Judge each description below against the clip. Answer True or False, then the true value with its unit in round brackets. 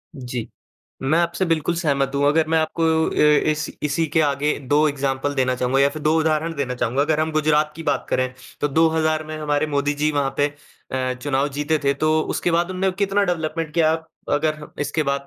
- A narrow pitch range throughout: True (2.2 semitones)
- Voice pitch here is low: False (150 Hz)